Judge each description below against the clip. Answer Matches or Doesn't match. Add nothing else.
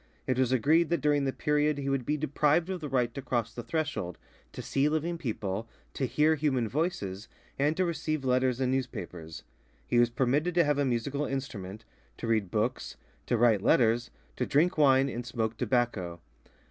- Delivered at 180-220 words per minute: Matches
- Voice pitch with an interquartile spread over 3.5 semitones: Matches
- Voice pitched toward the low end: Matches